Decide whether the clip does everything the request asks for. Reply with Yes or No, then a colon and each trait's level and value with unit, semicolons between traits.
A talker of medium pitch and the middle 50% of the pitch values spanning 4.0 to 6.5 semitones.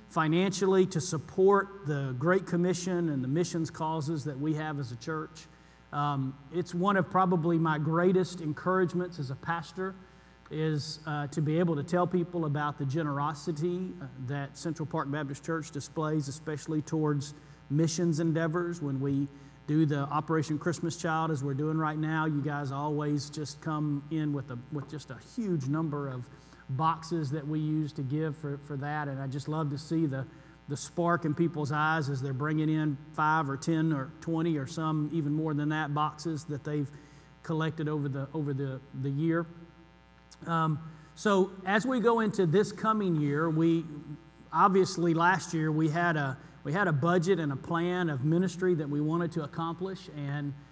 No: medium, 155 Hz; narrow, 2.4 semitones